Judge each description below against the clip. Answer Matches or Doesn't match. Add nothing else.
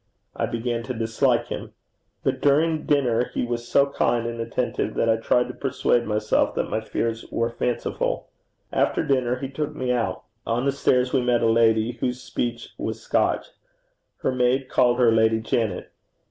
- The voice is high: Doesn't match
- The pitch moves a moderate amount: Doesn't match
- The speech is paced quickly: Doesn't match